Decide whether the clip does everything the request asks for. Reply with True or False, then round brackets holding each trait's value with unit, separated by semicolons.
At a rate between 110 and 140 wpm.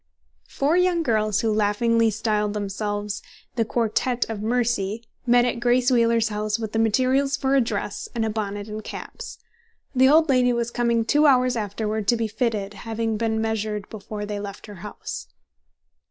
False (170 wpm)